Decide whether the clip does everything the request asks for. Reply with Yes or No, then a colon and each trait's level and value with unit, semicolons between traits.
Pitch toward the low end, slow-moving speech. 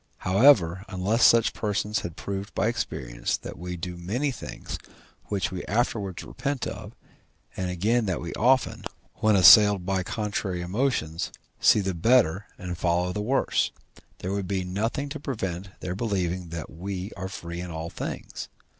No: very low, 95 Hz; average, 160 wpm